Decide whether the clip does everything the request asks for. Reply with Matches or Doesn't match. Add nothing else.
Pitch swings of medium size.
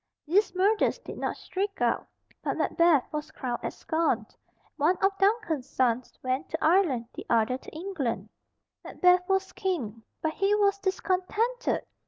Doesn't match